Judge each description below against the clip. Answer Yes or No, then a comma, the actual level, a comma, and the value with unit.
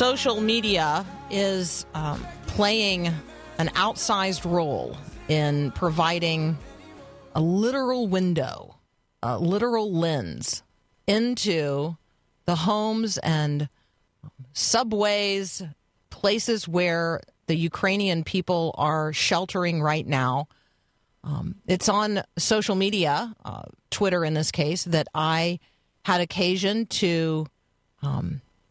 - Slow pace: Yes, slow, 95 wpm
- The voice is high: No, medium, 170 Hz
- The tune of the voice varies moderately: Yes, average, 4.6 semitones